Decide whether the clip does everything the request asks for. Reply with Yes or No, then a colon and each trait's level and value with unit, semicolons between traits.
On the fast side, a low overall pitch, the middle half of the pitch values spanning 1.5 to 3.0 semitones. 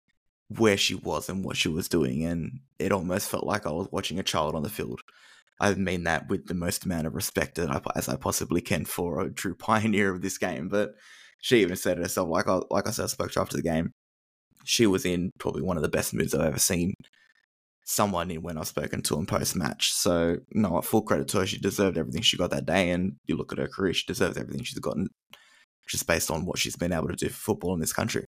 No: fast, 255 wpm; very low, 90 Hz; average, 3.5 semitones